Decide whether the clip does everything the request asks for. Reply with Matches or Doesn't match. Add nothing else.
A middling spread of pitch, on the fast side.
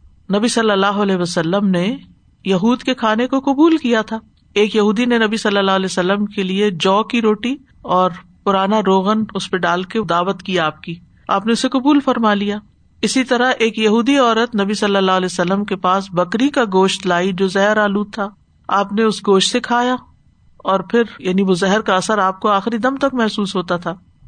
Matches